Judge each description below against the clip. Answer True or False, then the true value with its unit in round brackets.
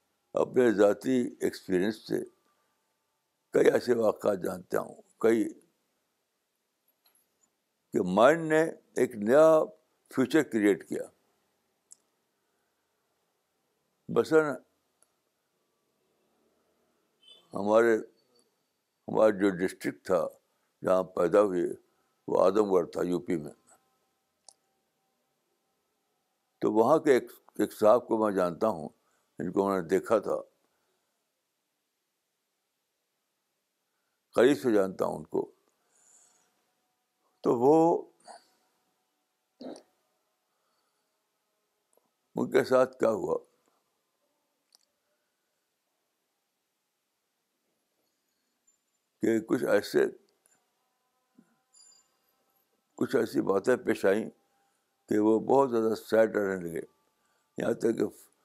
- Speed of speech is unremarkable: False (80 wpm)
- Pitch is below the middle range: False (155 Hz)